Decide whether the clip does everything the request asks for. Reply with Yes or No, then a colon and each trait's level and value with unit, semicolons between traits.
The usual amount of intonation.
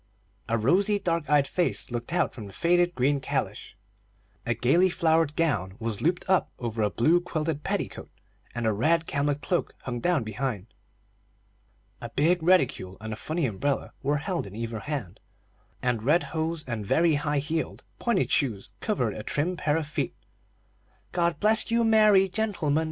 No: wide, 6.6 semitones